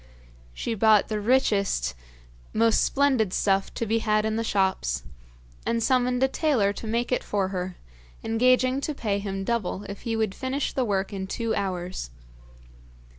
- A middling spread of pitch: Yes, average, 3.7 semitones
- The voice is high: Yes, high, 220 Hz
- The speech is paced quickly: No, average, 165 wpm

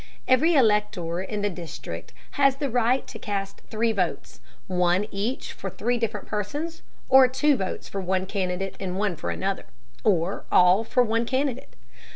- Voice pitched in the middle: No, high, 210 Hz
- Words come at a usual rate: Yes, average, 165 wpm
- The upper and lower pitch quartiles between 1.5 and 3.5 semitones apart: No, average, 4.9 semitones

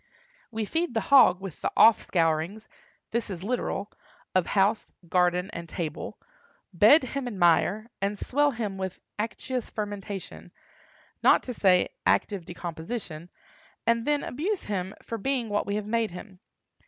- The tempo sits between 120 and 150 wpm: Yes, average, 145 wpm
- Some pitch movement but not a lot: Yes, average, 4.3 semitones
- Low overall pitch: No, high, 205 Hz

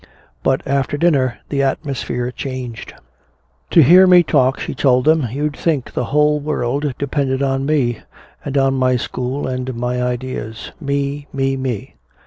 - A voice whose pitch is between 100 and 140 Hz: Yes, low, 135 Hz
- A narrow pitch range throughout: Yes, narrow, 2.2 semitones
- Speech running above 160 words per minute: No, average, 150 wpm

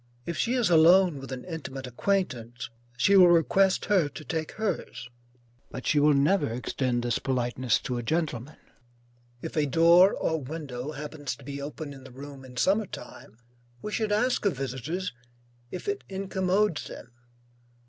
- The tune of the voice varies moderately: No, wide, 6.0 semitones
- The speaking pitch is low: No, medium, 150 Hz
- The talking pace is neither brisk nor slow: Yes, average, 165 wpm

